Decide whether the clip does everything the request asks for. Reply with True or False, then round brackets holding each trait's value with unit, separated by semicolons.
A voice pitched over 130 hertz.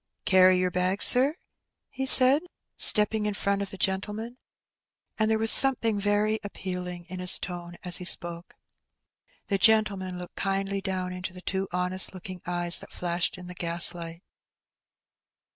True (185 Hz)